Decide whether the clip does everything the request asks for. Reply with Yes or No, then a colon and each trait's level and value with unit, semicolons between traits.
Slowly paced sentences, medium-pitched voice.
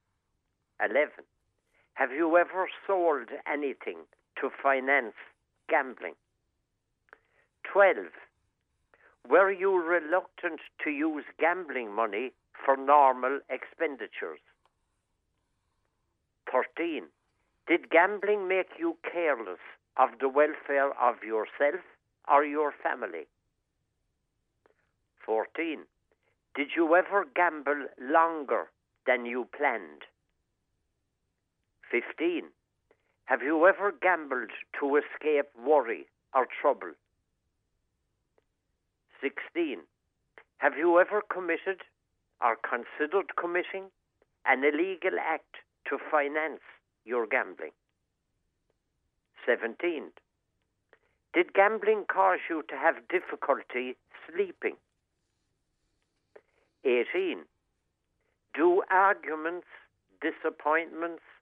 Yes: slow, 80 wpm; medium, 160 Hz